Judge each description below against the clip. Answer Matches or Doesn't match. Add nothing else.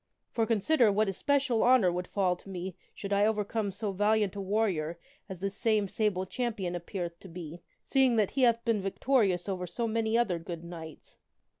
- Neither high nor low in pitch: Doesn't match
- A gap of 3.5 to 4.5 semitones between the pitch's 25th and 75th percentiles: Matches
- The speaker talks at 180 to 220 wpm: Matches